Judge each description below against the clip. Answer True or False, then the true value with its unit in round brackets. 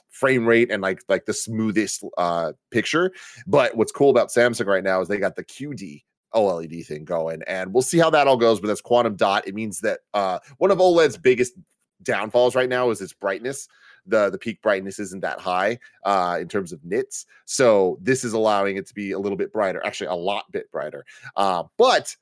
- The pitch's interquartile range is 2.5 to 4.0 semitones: False (4.6 semitones)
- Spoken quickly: True (215 wpm)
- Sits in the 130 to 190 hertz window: False (110 Hz)